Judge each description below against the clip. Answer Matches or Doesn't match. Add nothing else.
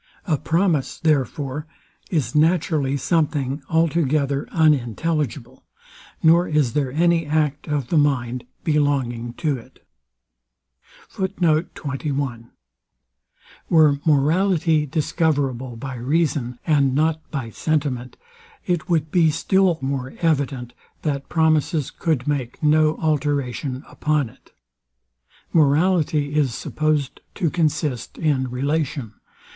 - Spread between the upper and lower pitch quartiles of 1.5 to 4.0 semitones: Matches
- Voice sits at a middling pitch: Matches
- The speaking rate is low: Matches